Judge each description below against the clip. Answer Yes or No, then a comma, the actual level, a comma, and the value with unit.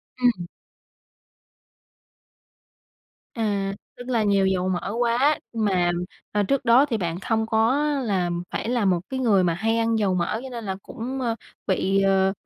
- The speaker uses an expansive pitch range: No, average, 3.7 semitones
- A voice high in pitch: Yes, high, 215 Hz